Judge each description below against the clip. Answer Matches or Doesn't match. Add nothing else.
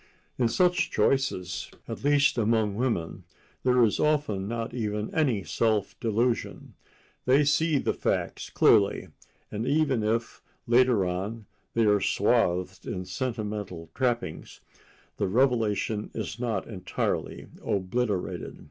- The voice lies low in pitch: Matches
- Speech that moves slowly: Matches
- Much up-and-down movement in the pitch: Doesn't match